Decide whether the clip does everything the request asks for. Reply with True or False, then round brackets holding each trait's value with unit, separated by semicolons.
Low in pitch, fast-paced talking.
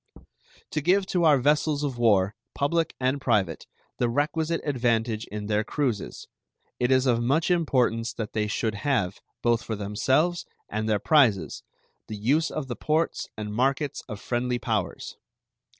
False (125 Hz; 155 wpm)